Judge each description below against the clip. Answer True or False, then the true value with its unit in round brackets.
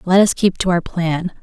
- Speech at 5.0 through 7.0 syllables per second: False (4.7 syllables/s)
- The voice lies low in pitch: False (180 Hz)